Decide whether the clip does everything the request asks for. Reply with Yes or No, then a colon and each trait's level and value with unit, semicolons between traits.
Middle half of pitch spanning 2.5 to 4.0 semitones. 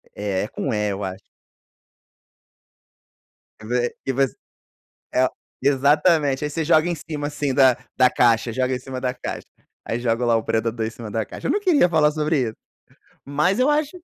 No: average, 4.7 semitones